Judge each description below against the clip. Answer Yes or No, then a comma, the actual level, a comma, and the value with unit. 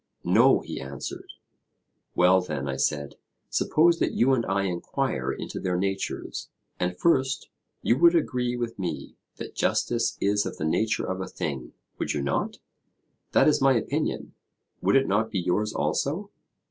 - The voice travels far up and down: Yes, wide, 6.8 semitones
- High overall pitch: No, low, 100 Hz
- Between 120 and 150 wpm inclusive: No, average, 160 wpm